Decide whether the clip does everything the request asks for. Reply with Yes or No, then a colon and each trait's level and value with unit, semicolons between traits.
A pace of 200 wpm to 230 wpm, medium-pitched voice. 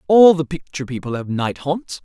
Yes: fast, 205 wpm; medium, 150 Hz